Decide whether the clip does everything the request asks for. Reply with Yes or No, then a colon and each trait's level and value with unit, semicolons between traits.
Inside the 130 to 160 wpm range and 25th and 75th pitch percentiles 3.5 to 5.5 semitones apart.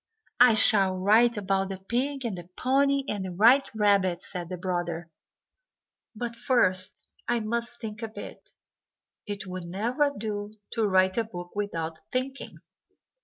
Yes: average, 150 wpm; average, 4.2 semitones